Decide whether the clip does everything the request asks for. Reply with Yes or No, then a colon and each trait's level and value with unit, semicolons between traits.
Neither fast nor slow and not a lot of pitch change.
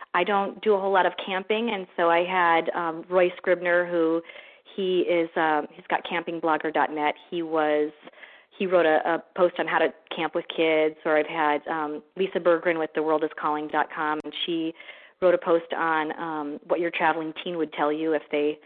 Yes: average, 195 wpm; narrow, 2.3 semitones